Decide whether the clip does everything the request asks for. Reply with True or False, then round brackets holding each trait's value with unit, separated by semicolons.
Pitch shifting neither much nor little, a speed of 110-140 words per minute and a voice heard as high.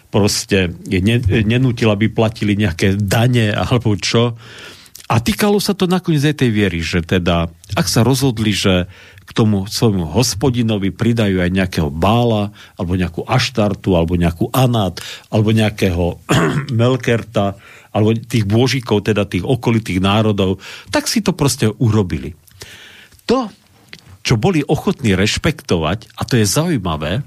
False (3.9 semitones; 135 wpm; 110 Hz)